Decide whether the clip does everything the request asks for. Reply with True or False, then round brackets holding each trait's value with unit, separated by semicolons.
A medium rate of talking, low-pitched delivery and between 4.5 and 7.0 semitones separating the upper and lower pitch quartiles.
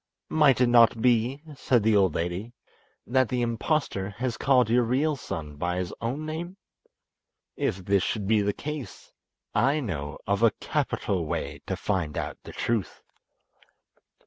True (155 wpm; 115 Hz; 5.0 semitones)